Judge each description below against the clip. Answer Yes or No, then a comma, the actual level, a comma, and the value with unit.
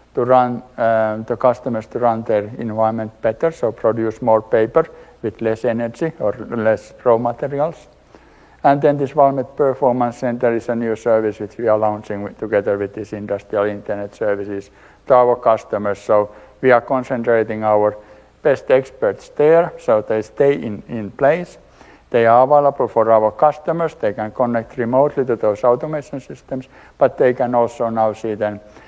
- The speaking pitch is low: Yes, low, 115 Hz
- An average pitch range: Yes, average, 3.5 semitones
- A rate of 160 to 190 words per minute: Yes, average, 165 wpm